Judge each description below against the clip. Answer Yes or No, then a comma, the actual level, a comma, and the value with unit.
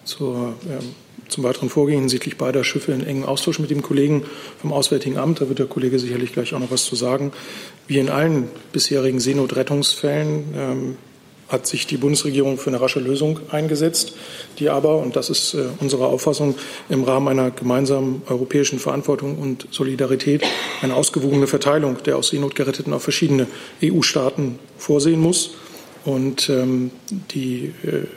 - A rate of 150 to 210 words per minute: Yes, average, 160 wpm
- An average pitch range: No, narrow, 2.1 semitones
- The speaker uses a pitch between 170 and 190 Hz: No, medium, 140 Hz